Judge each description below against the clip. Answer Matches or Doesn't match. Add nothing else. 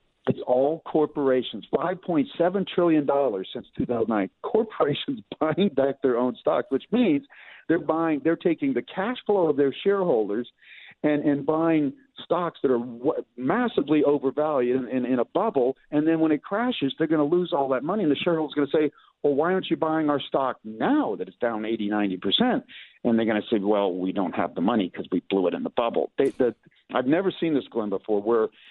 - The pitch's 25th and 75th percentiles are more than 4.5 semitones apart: Matches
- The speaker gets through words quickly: Matches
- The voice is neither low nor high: Matches